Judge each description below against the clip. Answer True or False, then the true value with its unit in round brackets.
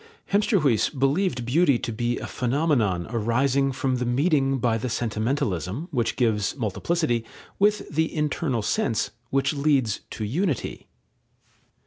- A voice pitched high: False (130 Hz)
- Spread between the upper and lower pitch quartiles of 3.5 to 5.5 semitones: True (4.5 semitones)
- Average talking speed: False (125 wpm)